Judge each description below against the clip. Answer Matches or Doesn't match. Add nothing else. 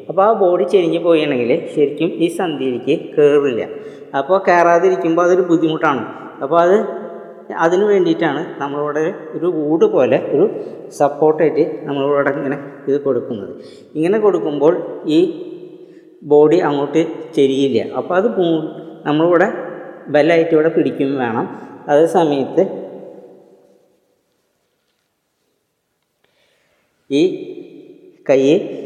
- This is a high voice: Doesn't match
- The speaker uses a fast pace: Doesn't match